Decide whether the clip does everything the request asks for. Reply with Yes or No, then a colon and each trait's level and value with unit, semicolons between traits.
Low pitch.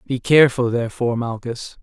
Yes: low, 120 Hz